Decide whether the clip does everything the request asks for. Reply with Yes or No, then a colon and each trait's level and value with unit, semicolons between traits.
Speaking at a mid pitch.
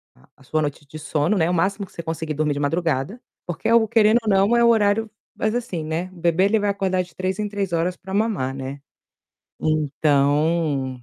Yes: medium, 175 Hz